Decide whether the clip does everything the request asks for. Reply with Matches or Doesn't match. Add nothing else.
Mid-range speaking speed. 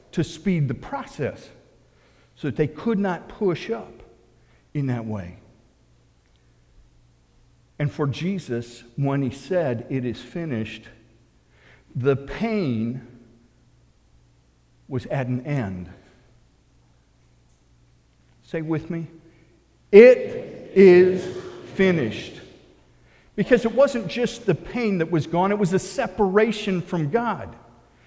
Doesn't match